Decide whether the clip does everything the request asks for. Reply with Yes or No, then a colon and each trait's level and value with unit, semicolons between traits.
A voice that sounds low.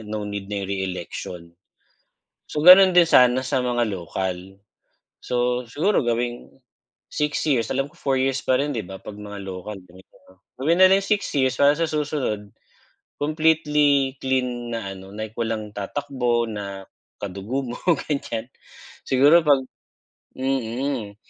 Yes: low, 125 Hz